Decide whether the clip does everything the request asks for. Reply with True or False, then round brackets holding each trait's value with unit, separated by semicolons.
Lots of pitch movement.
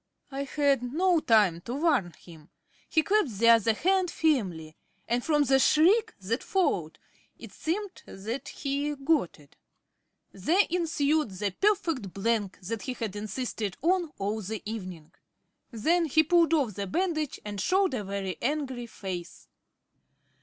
True (8.0 semitones)